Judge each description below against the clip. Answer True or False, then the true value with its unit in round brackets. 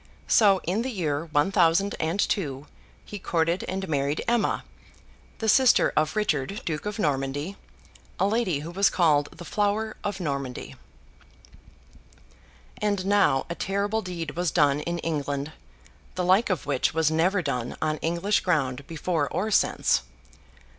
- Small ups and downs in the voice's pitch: False (5.2 semitones)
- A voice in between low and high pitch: True (170 Hz)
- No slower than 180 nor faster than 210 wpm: False (145 wpm)